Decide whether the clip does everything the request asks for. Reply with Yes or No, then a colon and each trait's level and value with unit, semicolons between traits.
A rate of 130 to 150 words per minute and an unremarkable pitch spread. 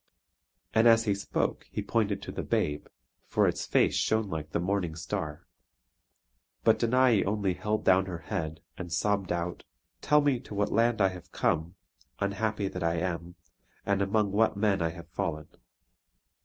No: average, 170 wpm; average, 3.9 semitones